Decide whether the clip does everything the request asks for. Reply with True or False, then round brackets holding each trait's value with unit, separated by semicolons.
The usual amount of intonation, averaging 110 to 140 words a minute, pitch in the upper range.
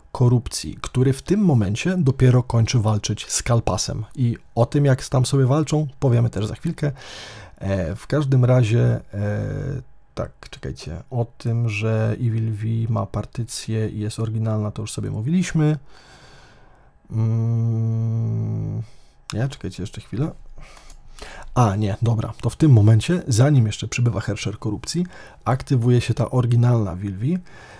False (3.5 semitones; 135 wpm; 115 Hz)